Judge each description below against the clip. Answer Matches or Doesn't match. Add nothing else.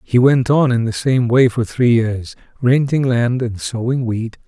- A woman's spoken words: Doesn't match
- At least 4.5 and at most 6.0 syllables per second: Doesn't match